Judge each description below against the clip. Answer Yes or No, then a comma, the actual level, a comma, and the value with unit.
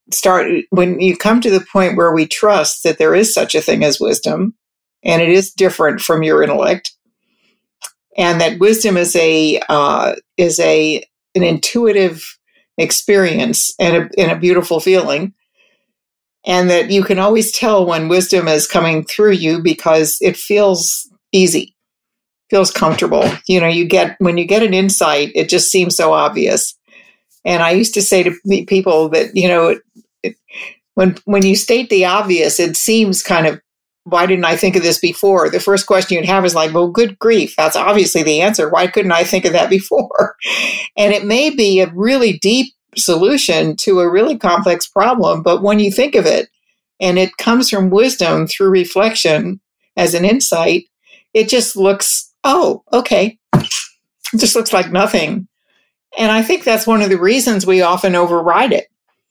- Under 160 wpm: No, average, 175 wpm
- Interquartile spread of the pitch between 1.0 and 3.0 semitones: No, average, 3.5 semitones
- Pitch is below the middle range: No, high, 190 Hz